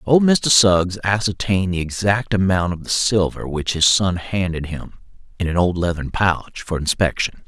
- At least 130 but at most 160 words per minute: No, average, 175 wpm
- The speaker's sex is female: No, male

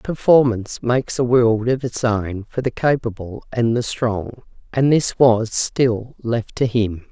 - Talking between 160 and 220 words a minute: Yes, average, 170 wpm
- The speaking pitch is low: Yes, low, 120 Hz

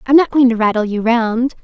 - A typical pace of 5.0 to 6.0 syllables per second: Yes, 5.5 syllables/s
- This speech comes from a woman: Yes, female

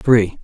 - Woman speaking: No, male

